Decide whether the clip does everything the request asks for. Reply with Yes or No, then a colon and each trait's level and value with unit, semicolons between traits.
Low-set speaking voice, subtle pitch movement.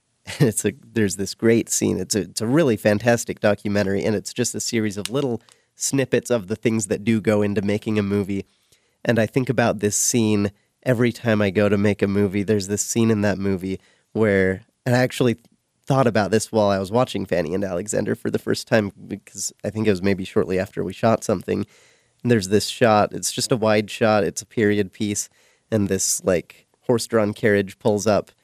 Yes: low, 105 Hz; narrow, 2.3 semitones